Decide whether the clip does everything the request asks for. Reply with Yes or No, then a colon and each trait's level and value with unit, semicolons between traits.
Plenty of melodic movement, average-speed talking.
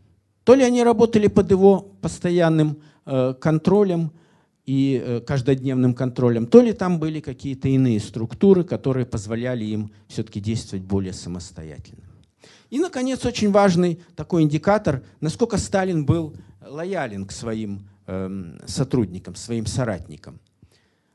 Yes: wide, 8.7 semitones; average, 120 wpm